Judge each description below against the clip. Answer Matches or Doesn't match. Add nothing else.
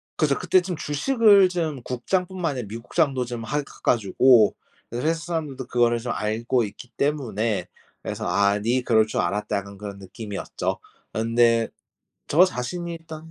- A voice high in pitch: Doesn't match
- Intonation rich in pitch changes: Matches